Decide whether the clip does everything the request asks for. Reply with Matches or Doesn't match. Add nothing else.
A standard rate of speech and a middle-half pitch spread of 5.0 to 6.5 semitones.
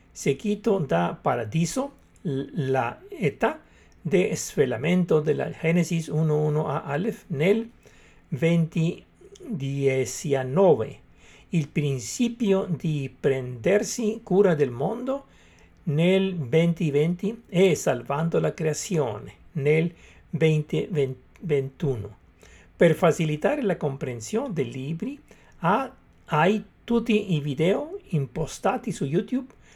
Doesn't match